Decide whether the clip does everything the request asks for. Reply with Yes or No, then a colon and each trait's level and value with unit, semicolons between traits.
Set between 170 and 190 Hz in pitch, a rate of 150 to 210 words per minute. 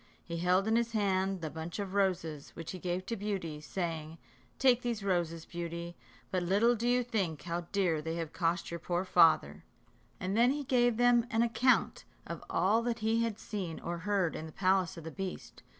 Yes: medium, 185 Hz; average, 200 wpm